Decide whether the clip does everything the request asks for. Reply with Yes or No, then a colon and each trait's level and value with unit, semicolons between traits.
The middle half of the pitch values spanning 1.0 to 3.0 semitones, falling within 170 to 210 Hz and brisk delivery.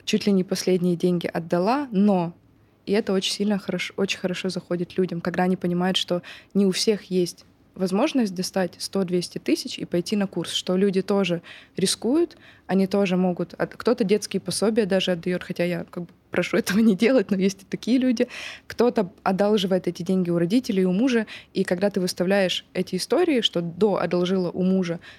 Yes: narrow, 2.4 semitones; high, 190 Hz; fast, 180 wpm